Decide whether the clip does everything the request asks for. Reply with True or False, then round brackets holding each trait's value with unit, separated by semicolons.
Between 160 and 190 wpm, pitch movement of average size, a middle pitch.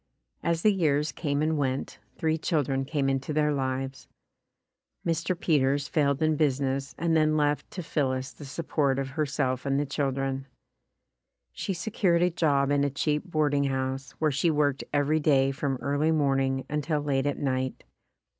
False (165 wpm; 2.3 semitones; 145 Hz)